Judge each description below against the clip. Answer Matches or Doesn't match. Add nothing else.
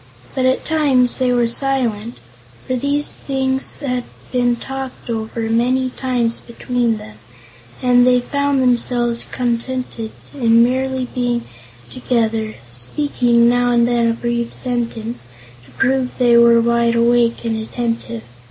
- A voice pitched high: Matches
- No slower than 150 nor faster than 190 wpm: Doesn't match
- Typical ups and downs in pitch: Doesn't match